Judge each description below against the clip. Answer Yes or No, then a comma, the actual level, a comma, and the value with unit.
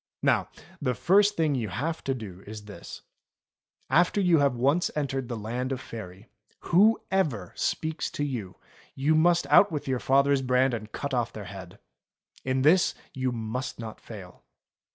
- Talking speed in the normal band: Yes, average, 165 wpm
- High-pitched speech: No, low, 130 Hz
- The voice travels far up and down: Yes, wide, 5.7 semitones